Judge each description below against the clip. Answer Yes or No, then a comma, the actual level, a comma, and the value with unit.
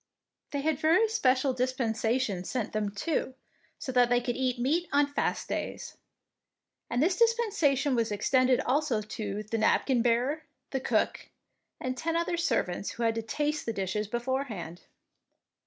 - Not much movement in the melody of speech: No, average, 4.4 semitones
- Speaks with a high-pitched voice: Yes, very high, 255 Hz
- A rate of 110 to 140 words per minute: No, average, 155 wpm